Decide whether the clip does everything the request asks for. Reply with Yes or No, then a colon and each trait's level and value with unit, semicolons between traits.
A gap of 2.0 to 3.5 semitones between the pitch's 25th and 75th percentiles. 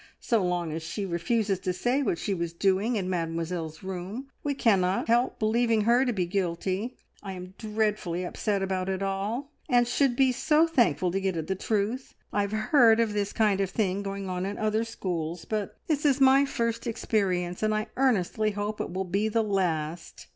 No: average, 4.0 semitones